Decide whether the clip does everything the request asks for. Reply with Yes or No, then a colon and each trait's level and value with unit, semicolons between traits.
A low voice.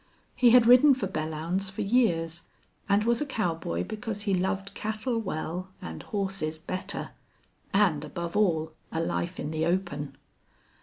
No: high, 190 Hz